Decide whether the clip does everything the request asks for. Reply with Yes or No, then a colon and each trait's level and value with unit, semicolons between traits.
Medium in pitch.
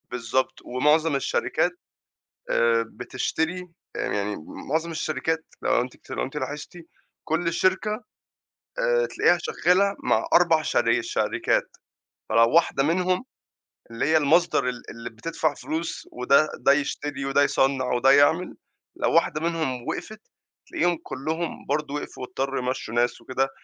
Yes: medium, 150 Hz